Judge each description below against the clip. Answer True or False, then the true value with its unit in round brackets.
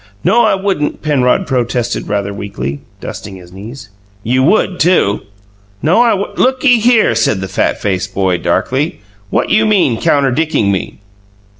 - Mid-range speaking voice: False (130 Hz)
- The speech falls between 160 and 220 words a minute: False (150 wpm)